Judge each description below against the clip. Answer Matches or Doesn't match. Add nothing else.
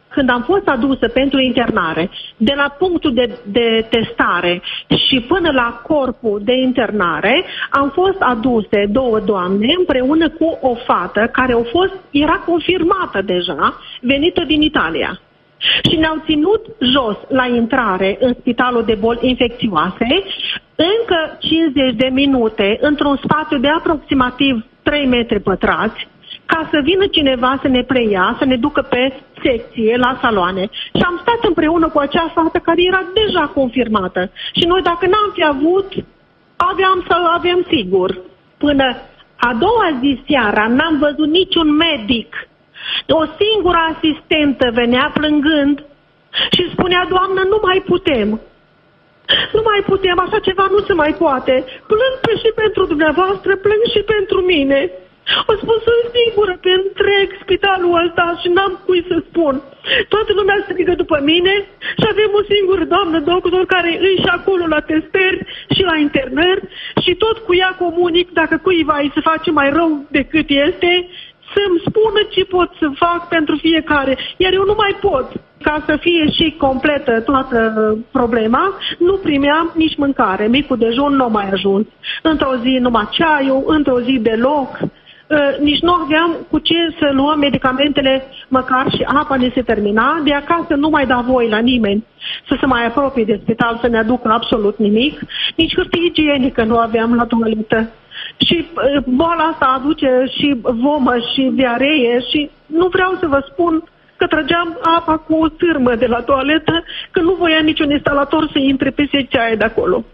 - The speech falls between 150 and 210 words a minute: Matches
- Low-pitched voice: Doesn't match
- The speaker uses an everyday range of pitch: Doesn't match